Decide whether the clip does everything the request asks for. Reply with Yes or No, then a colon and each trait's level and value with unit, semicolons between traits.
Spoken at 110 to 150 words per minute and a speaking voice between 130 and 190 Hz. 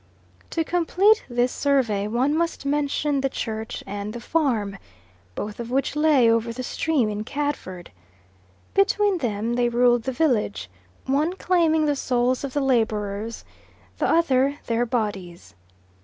No: average, 140 wpm; very high, 250 Hz